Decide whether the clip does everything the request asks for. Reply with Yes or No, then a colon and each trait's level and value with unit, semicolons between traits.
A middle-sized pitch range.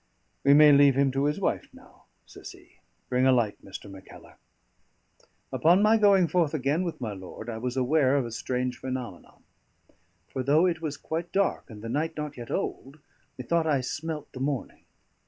Yes: average, 4.1 semitones